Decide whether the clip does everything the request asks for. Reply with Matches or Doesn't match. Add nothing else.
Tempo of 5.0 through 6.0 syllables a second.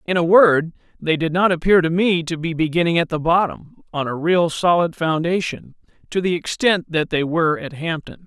Matches